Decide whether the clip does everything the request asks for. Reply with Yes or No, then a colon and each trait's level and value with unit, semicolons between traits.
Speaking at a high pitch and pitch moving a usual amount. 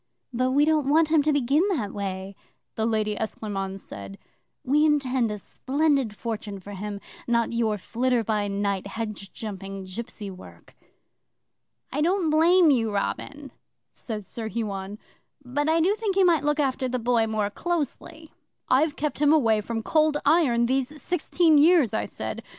No: high, 240 Hz; wide, 6.1 semitones